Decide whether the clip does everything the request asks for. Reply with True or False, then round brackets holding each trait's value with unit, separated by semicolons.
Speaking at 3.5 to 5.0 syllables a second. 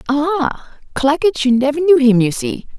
True (4.4 syllables/s)